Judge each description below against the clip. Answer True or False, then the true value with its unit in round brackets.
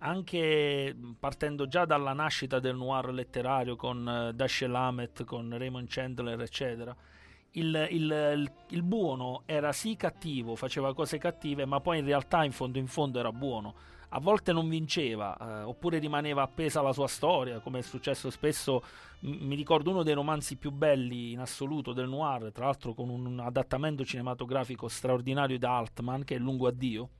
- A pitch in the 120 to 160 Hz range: True (135 Hz)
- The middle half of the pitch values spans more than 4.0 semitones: False (3.3 semitones)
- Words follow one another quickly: True (175 wpm)